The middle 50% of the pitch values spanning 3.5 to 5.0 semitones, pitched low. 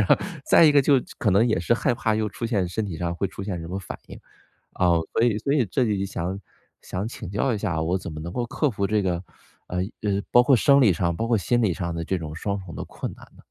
Yes: average, 4.6 semitones; low, 100 Hz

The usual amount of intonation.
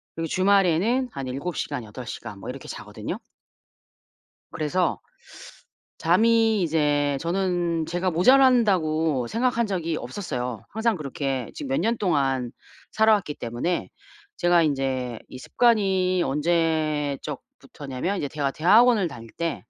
No: wide, 6.0 semitones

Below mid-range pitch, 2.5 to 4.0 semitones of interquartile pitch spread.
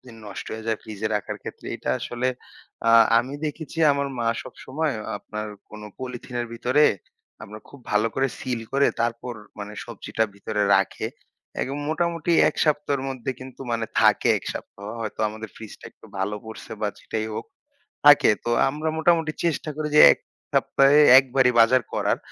No: low, 125 Hz; average, 4.5 semitones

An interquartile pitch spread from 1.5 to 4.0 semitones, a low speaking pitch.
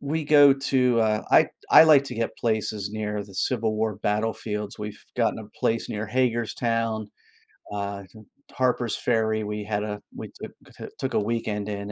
Yes: narrow, 2.6 semitones; low, 110 Hz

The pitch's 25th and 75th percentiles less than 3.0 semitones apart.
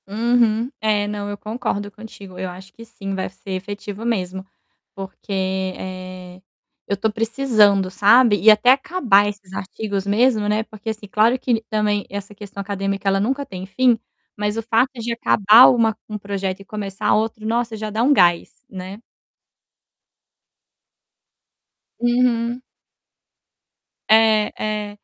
Yes: narrow, 2.5 semitones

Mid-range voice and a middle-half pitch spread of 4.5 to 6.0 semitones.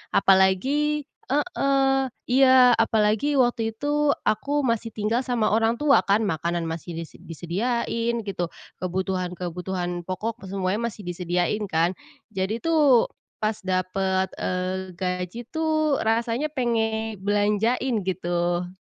No: high, 215 Hz; average, 5.1 semitones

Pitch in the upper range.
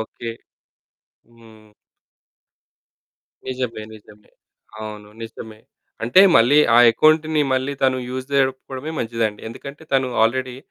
No: low, 125 Hz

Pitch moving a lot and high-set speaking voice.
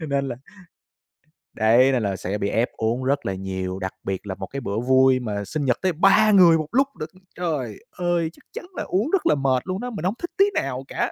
No: wide, 8.1 semitones; low, 130 Hz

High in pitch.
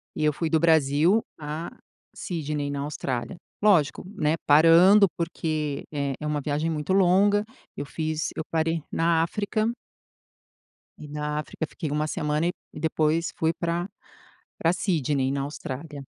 No: medium, 155 Hz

